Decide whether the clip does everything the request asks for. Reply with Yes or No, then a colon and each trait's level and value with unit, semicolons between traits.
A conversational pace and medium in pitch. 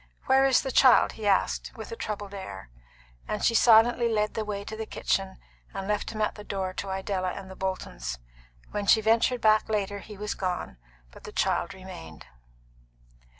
No: average, 190 wpm; high, 205 Hz